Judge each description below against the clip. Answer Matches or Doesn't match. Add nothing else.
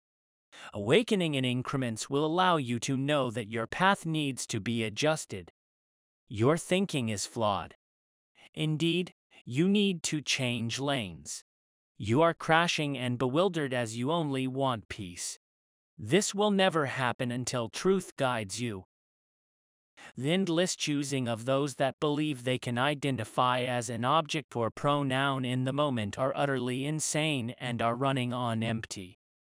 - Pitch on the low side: Matches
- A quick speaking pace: Doesn't match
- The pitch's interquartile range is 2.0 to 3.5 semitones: Doesn't match